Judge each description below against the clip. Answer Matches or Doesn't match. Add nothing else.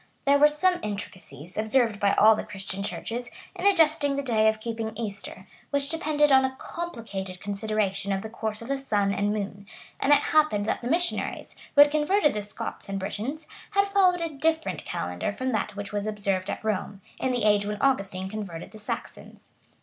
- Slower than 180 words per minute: Doesn't match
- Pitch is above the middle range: Matches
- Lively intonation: Matches